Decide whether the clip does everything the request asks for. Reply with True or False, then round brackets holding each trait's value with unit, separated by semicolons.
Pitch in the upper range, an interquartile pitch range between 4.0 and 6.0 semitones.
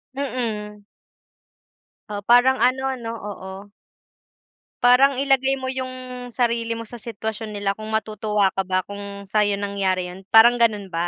False (220 Hz; 3.6 semitones)